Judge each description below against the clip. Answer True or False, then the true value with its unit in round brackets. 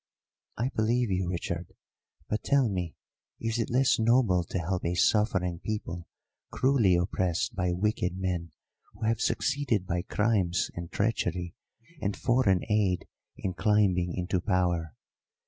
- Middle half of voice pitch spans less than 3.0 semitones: False (3.9 semitones)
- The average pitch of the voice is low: True (95 Hz)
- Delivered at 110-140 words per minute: True (135 wpm)